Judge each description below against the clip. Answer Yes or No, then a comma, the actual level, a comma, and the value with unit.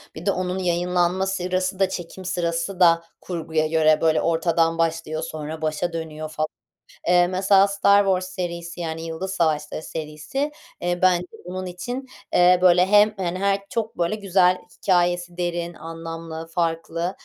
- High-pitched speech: No, medium, 175 Hz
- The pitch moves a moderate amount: No, narrow, 2.1 semitones